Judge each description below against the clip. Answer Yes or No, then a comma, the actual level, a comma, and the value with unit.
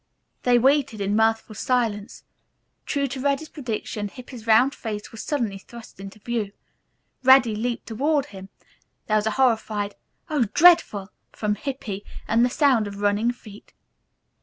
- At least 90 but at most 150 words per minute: Yes, average, 145 wpm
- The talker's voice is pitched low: No, high, 225 Hz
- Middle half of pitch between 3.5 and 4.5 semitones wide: Yes, average, 3.9 semitones